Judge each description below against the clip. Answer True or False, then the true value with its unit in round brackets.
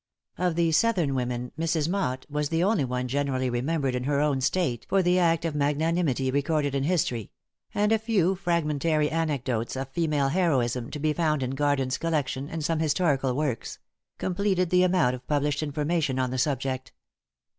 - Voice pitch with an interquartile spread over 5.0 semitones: False (4.0 semitones)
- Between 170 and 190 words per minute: True (175 wpm)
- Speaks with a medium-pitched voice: True (150 Hz)